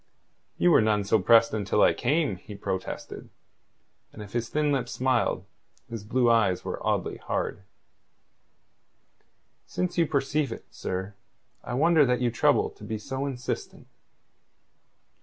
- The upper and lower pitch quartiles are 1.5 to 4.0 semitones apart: No, average, 4.8 semitones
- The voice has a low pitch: Yes, low, 120 Hz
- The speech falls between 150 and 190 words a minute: No, average, 140 wpm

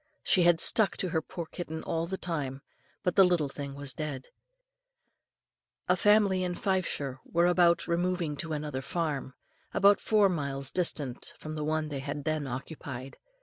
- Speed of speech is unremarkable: Yes, average, 160 wpm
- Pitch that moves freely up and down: No, average, 4.0 semitones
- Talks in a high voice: No, medium, 160 Hz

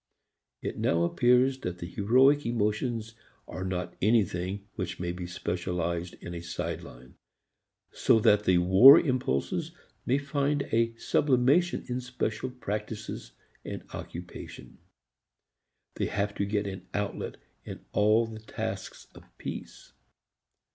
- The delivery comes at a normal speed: No, slow, 125 wpm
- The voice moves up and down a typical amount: No, wide, 5.7 semitones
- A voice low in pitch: Yes, low, 105 Hz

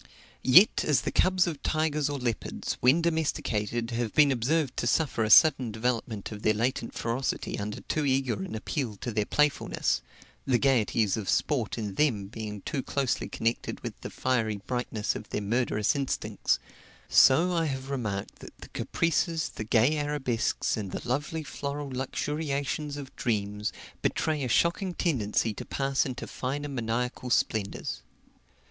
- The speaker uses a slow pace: No, average, 155 wpm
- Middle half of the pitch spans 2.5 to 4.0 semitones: No, average, 4.8 semitones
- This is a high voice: No, low, 130 Hz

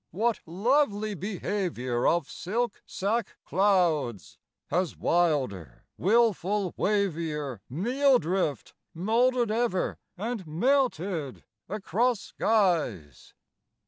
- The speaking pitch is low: No, high, 190 Hz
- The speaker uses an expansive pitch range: Yes, wide, 6.1 semitones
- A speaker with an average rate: No, slow, 80 wpm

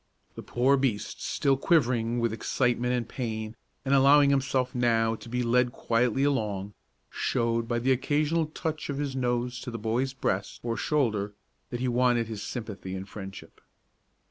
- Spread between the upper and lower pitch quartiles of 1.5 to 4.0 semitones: Yes, average, 2.8 semitones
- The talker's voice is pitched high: No, low, 120 Hz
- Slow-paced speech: No, average, 165 wpm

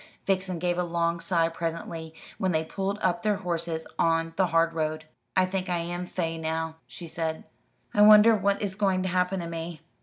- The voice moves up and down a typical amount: No, narrow, 2.3 semitones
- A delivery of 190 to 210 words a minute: Yes, average, 195 wpm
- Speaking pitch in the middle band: Yes, medium, 170 Hz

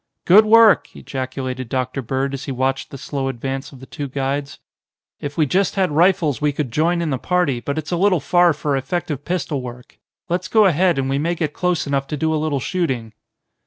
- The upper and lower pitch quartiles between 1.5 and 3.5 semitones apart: No, average, 4.5 semitones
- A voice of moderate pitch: Yes, medium, 145 Hz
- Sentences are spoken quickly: Yes, fast, 215 wpm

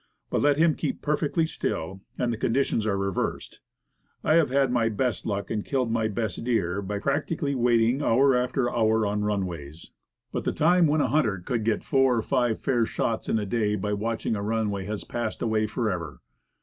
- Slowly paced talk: No, average, 195 wpm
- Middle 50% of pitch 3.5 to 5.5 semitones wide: Yes, average, 4.2 semitones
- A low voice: Yes, low, 115 Hz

